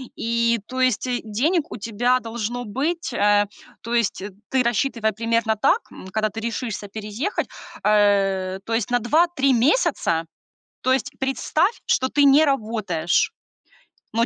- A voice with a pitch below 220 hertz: No, high, 230 Hz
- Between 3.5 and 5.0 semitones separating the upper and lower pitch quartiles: Yes, average, 3.9 semitones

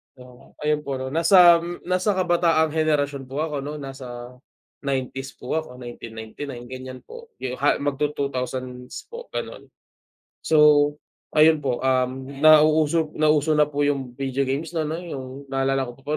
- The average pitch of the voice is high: No, medium, 145 Hz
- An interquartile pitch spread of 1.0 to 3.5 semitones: Yes, average, 3.1 semitones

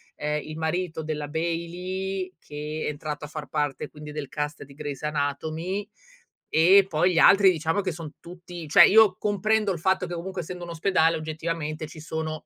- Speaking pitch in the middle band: Yes, medium, 160 Hz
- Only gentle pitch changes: No, average, 3.1 semitones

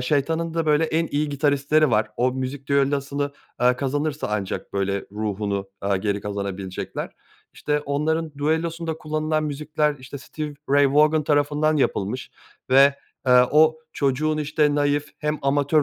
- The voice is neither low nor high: Yes, medium, 145 Hz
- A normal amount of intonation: Yes, average, 3.0 semitones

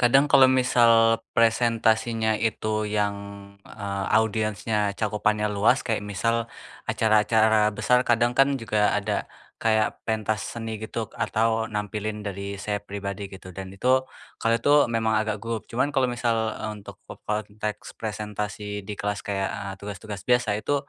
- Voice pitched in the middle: No, low, 110 Hz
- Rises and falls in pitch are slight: Yes, narrow, 1.9 semitones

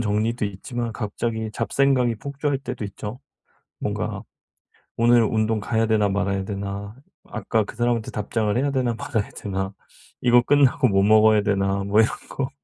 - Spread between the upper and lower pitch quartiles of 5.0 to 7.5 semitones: No, average, 3.0 semitones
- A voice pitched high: No, low, 110 Hz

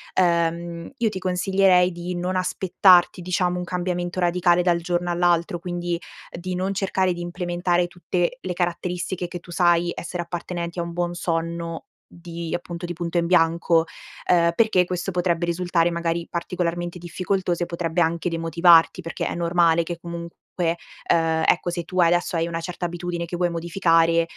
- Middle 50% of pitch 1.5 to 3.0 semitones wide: No, narrow, 1.0 semitones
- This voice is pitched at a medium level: Yes, medium, 175 Hz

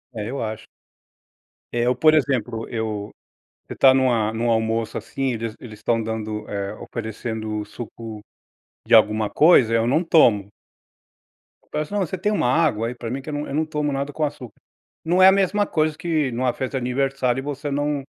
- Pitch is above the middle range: No, low, 125 Hz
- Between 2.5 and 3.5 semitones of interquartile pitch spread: No, average, 4.8 semitones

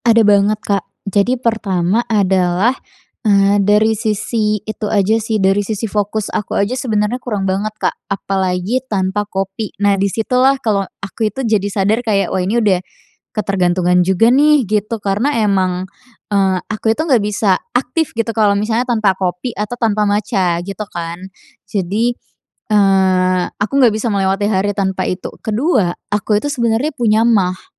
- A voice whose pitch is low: No, high, 210 Hz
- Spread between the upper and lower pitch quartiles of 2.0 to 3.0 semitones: Yes, narrow, 2.6 semitones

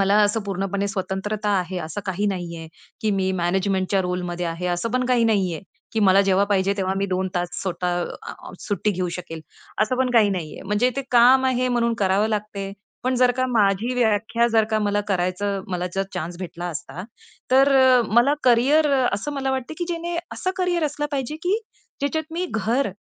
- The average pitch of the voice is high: Yes, high, 205 Hz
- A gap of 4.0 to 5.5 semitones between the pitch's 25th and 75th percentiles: Yes, average, 5.1 semitones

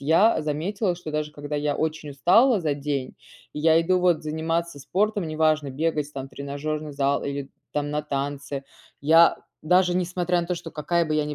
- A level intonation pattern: No, average, 3.0 semitones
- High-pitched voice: No, medium, 155 Hz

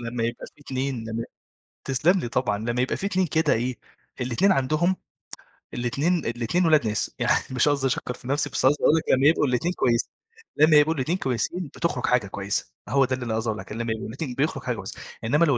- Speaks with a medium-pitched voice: No, low, 130 Hz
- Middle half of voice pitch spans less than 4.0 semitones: No, average, 4.7 semitones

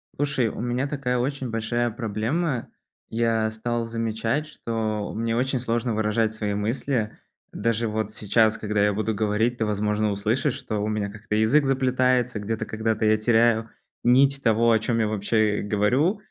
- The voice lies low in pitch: Yes, low, 115 Hz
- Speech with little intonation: Yes, narrow, 2.3 semitones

